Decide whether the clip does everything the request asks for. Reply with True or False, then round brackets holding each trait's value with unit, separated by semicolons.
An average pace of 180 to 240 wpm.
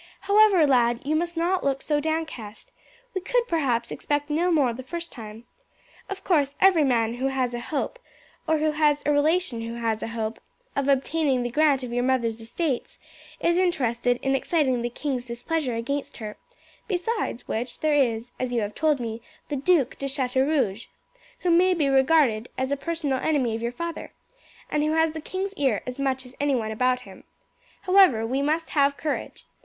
True (185 wpm)